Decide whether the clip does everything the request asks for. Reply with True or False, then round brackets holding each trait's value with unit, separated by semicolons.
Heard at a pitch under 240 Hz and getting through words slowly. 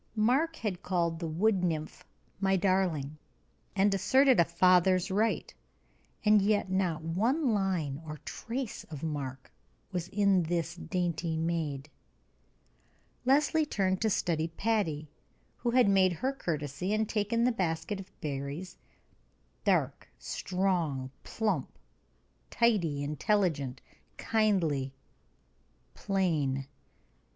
True (185 Hz; 110 wpm)